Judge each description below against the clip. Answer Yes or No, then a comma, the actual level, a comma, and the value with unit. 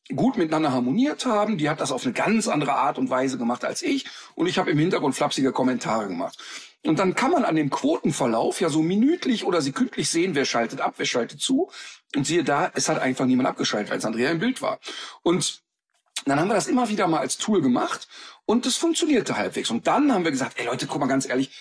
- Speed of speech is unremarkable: No, fast, 230 wpm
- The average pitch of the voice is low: No, medium, 170 Hz